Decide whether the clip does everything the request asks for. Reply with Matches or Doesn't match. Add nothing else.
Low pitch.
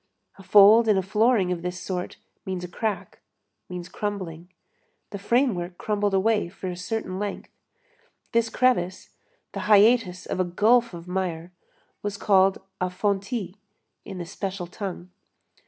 Doesn't match